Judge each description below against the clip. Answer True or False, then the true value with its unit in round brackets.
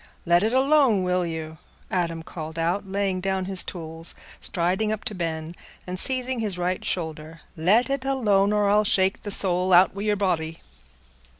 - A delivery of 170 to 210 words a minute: True (175 wpm)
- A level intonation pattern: False (3.6 semitones)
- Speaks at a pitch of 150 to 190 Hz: True (185 Hz)